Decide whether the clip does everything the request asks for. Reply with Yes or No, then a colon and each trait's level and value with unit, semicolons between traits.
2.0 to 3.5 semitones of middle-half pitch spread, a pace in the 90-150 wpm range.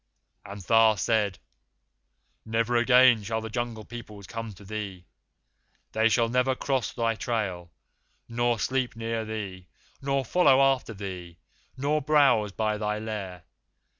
Yes: narrow, 2.6 semitones; slow, 135 wpm